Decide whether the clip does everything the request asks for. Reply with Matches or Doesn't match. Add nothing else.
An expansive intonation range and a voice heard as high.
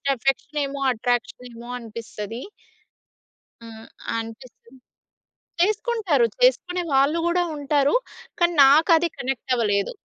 Matches